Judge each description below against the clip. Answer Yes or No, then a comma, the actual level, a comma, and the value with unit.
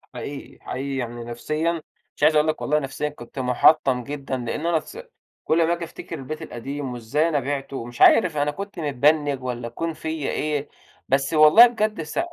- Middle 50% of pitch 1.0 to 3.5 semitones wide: Yes, average, 3.1 semitones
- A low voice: No, medium, 145 Hz